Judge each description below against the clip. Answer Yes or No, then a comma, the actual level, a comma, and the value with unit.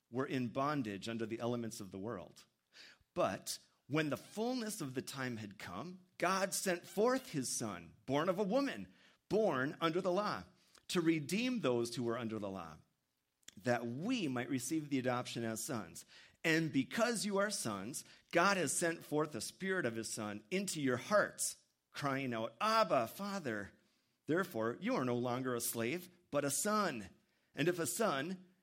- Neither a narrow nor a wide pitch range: No, wide, 8.1 semitones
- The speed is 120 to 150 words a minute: No, average, 170 wpm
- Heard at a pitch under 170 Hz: Yes, medium, 140 Hz